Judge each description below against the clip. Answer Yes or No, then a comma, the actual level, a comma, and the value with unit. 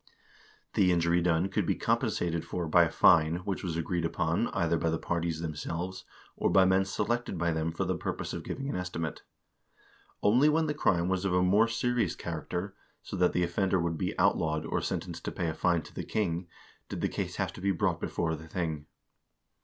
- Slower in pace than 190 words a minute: No, fast, 205 wpm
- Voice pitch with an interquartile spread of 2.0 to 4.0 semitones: Yes, narrow, 2.5 semitones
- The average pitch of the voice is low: Yes, very low, 85 Hz